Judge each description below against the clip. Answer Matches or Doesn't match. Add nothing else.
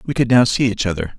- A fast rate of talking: Matches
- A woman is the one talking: Doesn't match